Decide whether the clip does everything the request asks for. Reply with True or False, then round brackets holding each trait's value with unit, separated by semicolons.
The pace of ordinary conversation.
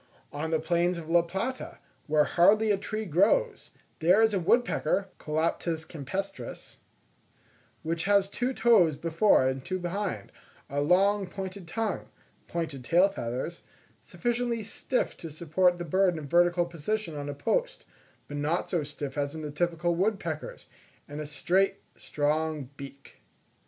True (150 wpm)